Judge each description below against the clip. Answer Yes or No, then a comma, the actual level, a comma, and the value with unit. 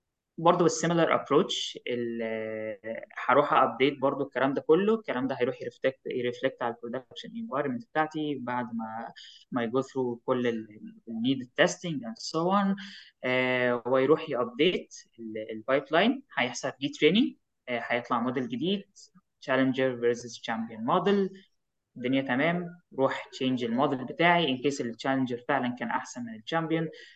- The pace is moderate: Yes, average, 125 wpm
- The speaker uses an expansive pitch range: Yes, wide, 5.7 semitones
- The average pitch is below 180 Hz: Yes, low, 135 Hz